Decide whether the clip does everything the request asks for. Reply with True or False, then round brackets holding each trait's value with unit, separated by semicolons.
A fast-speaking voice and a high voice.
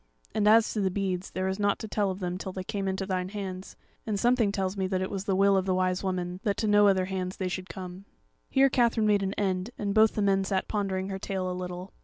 True (270 wpm; 195 Hz)